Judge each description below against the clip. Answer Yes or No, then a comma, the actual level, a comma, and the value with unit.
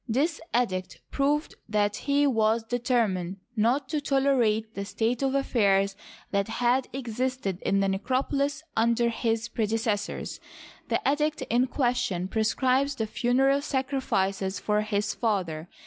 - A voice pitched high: Yes, high, 235 Hz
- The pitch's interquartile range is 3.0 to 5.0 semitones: Yes, average, 4.4 semitones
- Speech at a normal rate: No, slow, 130 wpm